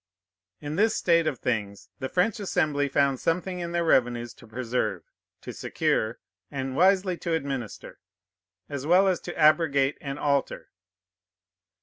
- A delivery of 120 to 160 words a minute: Yes, average, 140 wpm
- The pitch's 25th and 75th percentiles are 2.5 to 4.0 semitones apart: No, average, 4.7 semitones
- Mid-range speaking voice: Yes, medium, 145 Hz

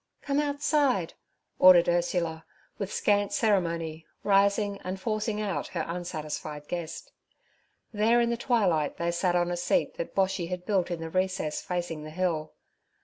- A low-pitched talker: No, medium, 180 Hz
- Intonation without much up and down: No, average, 3.4 semitones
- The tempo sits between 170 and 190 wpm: No, average, 150 wpm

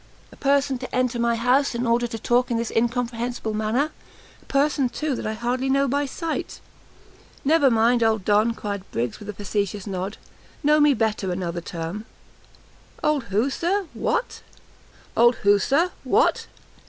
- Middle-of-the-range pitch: No, high, 235 Hz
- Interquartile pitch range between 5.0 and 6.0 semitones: No, average, 4.4 semitones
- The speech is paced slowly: No, average, 145 wpm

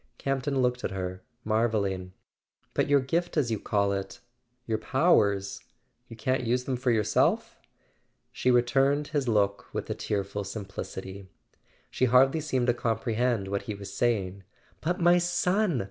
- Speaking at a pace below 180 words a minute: Yes, average, 160 wpm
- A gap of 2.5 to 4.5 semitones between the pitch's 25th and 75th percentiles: No, average, 5.0 semitones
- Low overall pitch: Yes, low, 120 Hz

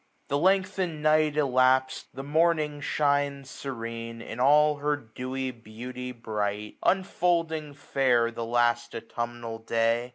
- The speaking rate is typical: No, slow, 120 wpm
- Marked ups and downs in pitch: No, average, 4.2 semitones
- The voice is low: Yes, low, 130 Hz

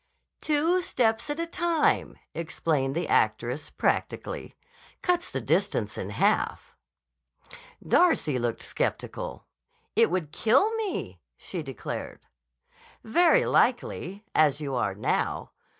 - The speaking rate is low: Yes, slow, 110 wpm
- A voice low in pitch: No, medium, 185 Hz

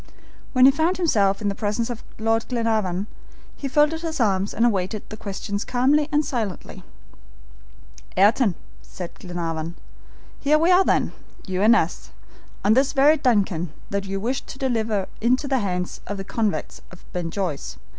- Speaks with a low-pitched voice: No, high, 220 Hz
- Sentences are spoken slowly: No, average, 165 wpm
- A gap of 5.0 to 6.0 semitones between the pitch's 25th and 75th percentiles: Yes, wide, 5.4 semitones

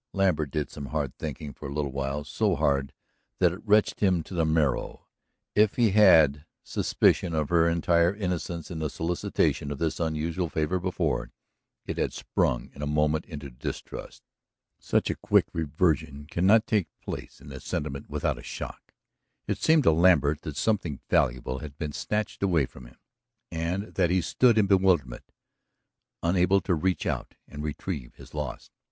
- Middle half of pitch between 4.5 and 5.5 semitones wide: No, average, 4.1 semitones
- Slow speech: No, average, 170 wpm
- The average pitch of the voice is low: Yes, very low, 80 Hz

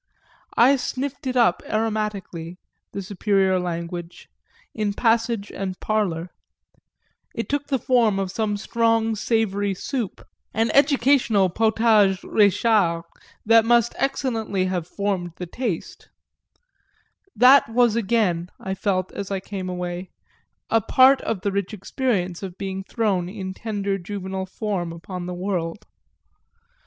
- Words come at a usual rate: No, slow, 125 wpm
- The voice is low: No, high, 200 Hz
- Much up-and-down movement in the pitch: No, average, 3.5 semitones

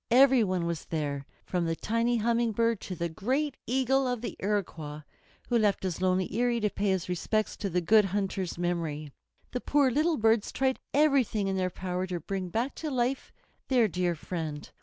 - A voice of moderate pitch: No, high, 205 Hz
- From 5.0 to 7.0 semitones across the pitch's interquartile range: Yes, wide, 5.4 semitones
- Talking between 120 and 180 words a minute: No, average, 190 wpm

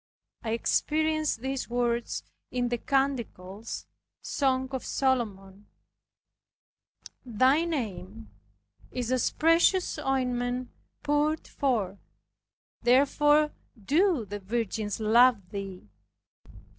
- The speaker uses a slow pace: Yes, slow, 85 wpm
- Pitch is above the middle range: Yes, high, 245 Hz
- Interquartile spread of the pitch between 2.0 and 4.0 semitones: No, average, 4.7 semitones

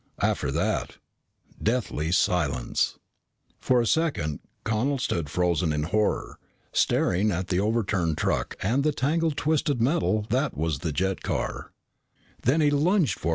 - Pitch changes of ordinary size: No, wide, 7.6 semitones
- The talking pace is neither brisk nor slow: No, slow, 125 wpm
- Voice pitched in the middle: No, low, 105 Hz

